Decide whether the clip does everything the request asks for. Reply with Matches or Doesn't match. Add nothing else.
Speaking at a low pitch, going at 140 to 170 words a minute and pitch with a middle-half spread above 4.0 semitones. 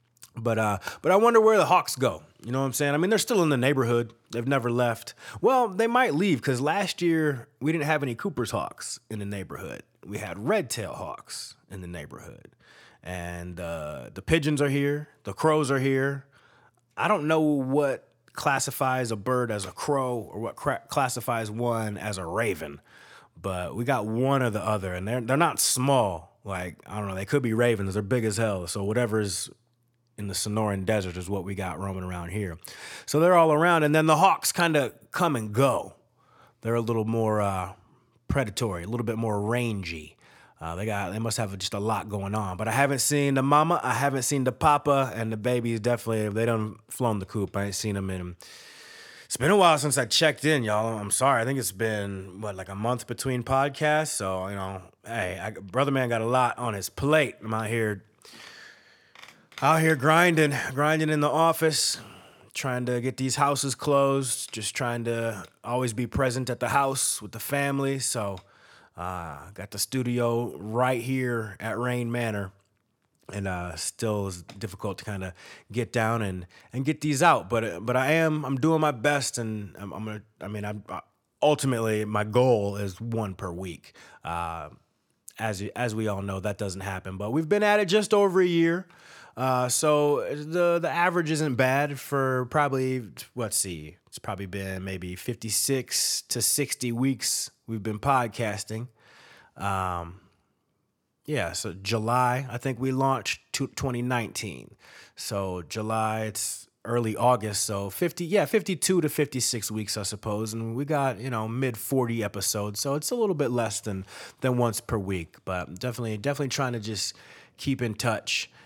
Doesn't match